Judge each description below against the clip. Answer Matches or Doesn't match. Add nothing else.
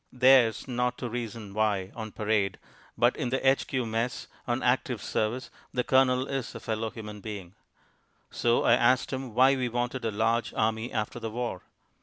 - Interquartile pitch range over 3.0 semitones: Doesn't match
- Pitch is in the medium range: Doesn't match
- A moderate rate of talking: Matches